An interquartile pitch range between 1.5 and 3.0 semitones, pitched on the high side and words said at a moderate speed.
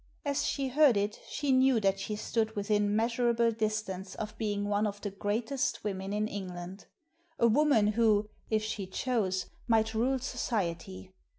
Yes: average, 2.7 semitones; high, 215 Hz; average, 165 wpm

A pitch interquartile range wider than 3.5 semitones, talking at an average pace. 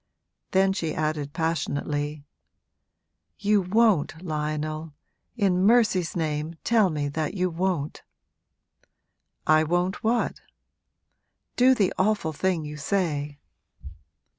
No: average, 4.1 semitones; slow, 100 wpm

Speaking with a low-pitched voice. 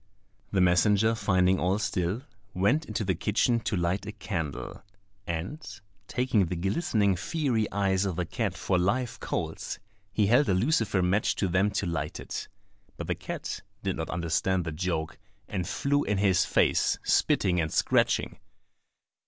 Yes: very low, 95 Hz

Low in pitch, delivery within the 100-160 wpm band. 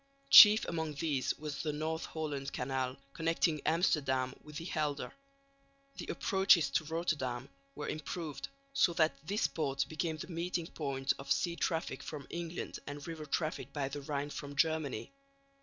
No: medium, 155 Hz; average, 155 wpm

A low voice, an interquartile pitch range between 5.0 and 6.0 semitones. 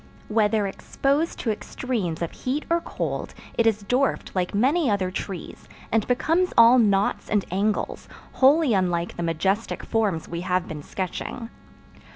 No: high, 210 Hz; average, 5.3 semitones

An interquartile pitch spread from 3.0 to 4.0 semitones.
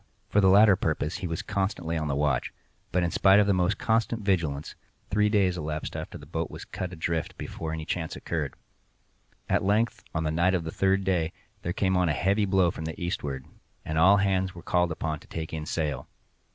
Yes: average, 3.4 semitones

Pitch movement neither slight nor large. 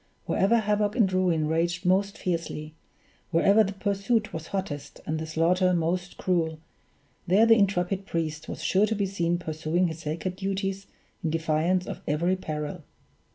Yes: average, 3.4 semitones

